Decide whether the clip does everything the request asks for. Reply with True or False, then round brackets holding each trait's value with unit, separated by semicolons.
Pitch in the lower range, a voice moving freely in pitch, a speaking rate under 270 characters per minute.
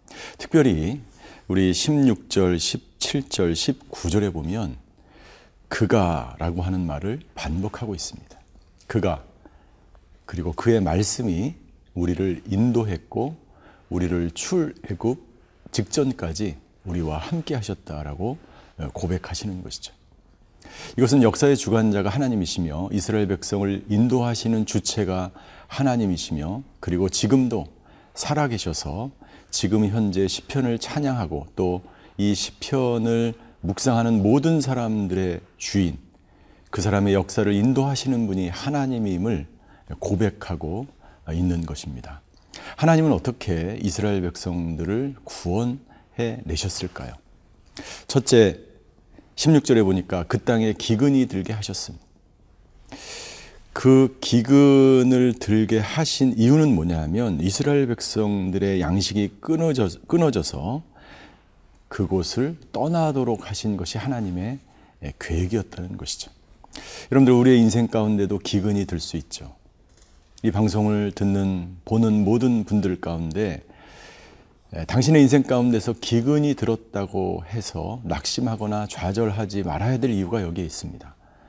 False (105 Hz; 4.9 semitones; 260 characters per minute)